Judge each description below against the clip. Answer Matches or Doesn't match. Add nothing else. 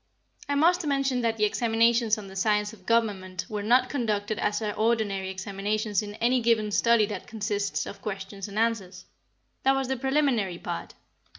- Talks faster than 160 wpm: Matches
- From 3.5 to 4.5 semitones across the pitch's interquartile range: Doesn't match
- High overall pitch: Matches